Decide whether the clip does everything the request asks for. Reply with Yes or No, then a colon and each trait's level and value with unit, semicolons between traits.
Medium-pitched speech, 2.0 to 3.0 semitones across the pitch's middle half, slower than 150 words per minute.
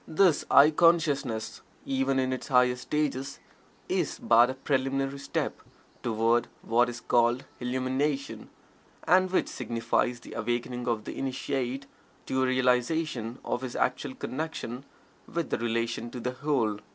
No: low, 130 Hz; narrow, 2.6 semitones; average, 140 wpm